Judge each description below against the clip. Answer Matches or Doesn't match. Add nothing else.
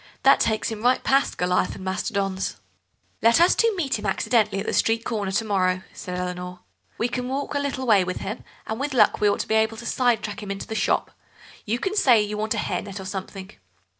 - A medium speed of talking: Doesn't match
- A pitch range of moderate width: Matches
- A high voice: Matches